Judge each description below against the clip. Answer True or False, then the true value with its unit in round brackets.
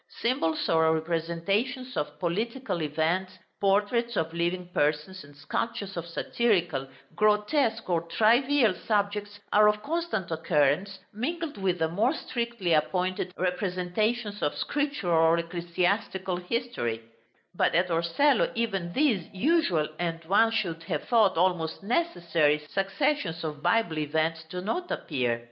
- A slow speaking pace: True (125 wpm)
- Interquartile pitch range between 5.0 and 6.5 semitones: True (5.4 semitones)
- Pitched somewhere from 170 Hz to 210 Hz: True (185 Hz)